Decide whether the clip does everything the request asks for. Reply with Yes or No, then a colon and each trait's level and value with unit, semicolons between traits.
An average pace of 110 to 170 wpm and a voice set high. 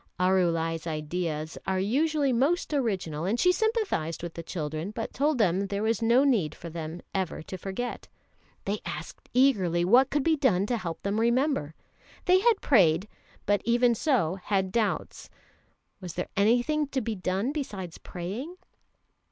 Yes: average, 160 wpm; high, 205 Hz